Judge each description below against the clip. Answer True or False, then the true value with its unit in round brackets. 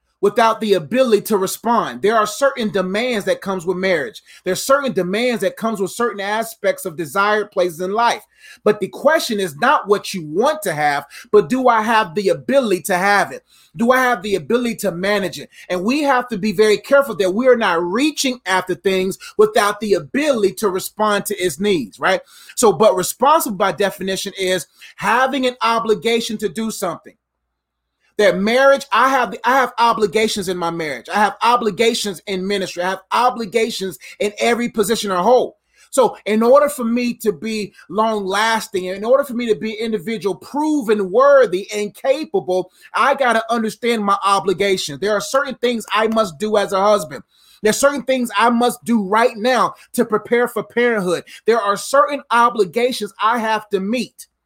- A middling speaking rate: True (185 wpm)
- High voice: True (215 Hz)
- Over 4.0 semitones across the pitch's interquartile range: False (3.6 semitones)